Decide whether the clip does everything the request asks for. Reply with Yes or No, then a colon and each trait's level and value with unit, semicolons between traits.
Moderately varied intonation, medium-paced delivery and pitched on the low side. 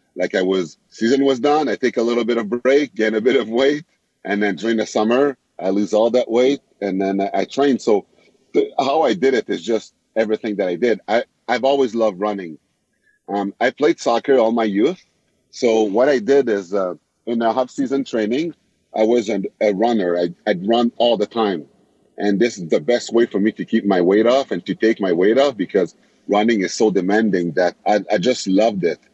No: average, 3.7 semitones; fast, 225 wpm; low, 115 Hz